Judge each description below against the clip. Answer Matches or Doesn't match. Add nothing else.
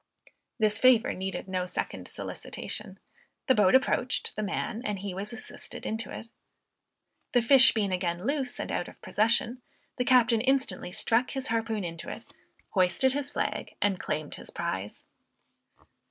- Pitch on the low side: Doesn't match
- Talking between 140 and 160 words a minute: Matches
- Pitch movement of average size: Matches